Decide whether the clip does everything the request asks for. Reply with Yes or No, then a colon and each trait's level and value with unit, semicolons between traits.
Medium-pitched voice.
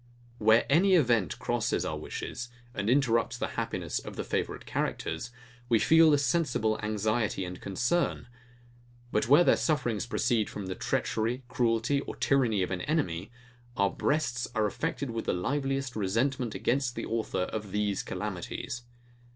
No: low, 115 Hz